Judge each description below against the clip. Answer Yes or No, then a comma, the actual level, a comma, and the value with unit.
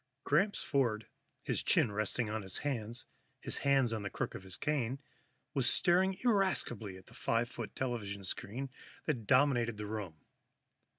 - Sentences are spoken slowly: No, average, 165 wpm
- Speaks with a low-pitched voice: Yes, low, 120 Hz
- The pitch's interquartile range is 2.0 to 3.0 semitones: No, average, 4.8 semitones